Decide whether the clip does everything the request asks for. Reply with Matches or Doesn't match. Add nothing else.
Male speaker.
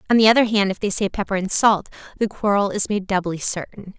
Doesn't match